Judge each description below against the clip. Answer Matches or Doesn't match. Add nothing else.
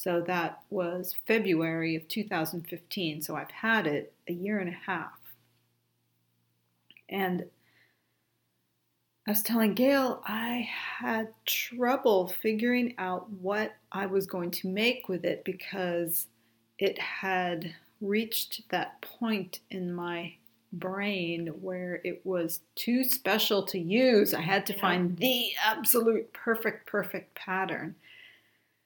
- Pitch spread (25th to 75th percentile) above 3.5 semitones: Matches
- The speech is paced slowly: Matches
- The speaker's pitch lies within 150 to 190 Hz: Matches